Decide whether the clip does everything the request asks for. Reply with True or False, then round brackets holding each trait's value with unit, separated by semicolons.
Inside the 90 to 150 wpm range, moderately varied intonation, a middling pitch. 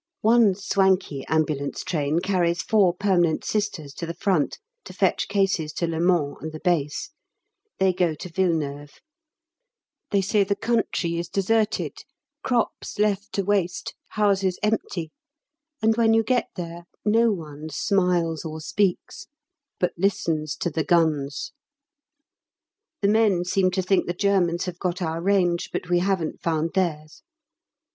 True (145 wpm; 3.6 semitones; 180 Hz)